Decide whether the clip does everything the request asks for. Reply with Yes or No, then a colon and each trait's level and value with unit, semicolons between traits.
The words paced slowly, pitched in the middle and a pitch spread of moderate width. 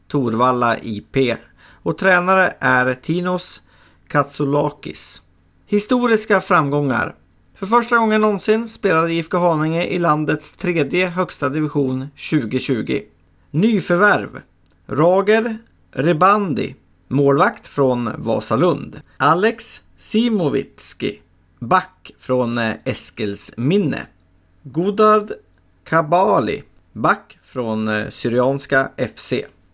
No: slow, 80 wpm; medium, 145 Hz; wide, 7.3 semitones